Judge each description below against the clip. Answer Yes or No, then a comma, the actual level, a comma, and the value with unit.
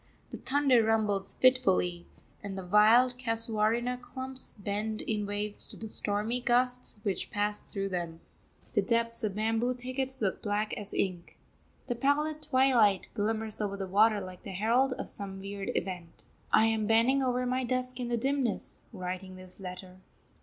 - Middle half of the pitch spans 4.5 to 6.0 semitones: No, average, 4.0 semitones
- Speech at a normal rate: Yes, average, 160 wpm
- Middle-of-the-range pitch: No, high, 220 Hz